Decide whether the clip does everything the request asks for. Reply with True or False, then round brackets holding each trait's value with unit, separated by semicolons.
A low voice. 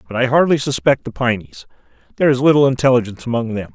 True (120 Hz)